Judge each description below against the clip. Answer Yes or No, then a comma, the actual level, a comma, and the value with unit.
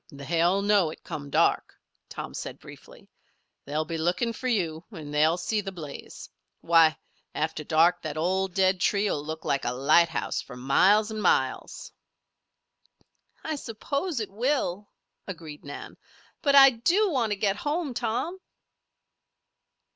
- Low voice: No, medium, 185 Hz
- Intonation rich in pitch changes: Yes, wide, 6.1 semitones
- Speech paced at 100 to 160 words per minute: Yes, average, 145 wpm